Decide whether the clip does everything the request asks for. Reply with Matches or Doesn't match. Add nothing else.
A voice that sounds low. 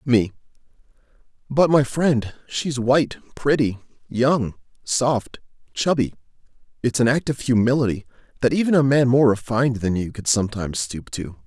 Matches